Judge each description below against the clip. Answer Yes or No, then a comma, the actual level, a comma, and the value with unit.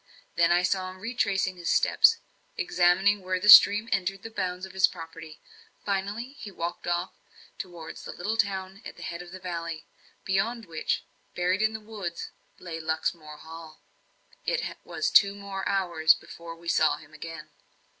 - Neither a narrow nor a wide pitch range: Yes, average, 3.1 semitones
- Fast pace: No, average, 165 wpm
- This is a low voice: No, medium, 185 Hz